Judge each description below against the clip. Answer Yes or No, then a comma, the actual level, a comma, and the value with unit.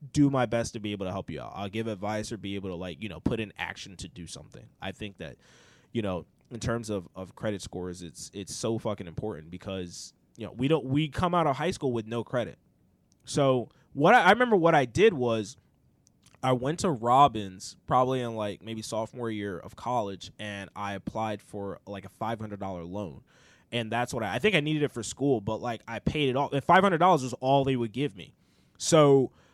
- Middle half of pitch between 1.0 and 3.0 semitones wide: No, average, 4.8 semitones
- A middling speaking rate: No, fast, 225 wpm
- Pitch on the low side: Yes, low, 115 Hz